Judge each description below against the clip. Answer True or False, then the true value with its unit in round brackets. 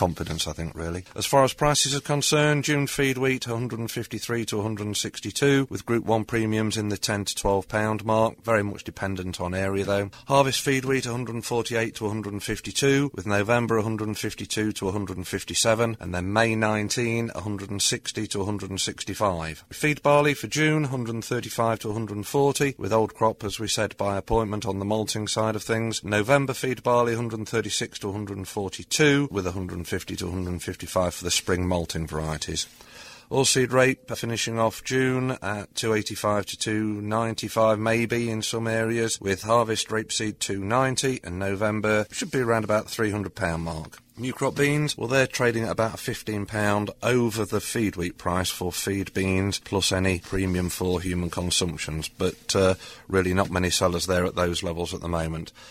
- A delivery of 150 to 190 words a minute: True (165 wpm)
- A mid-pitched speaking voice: False (110 Hz)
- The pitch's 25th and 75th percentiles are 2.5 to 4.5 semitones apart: True (3.4 semitones)